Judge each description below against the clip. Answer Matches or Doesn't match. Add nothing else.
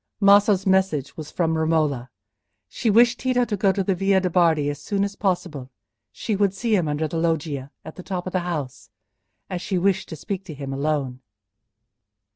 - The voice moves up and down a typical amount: Matches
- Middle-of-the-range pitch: Matches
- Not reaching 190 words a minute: Doesn't match